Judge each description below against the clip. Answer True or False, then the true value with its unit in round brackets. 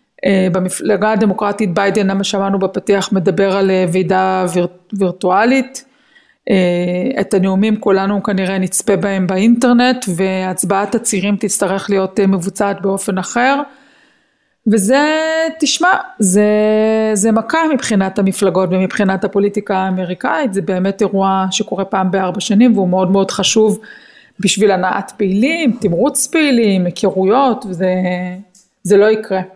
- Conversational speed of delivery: True (120 wpm)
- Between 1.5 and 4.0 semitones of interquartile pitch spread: True (2.8 semitones)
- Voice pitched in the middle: False (200 Hz)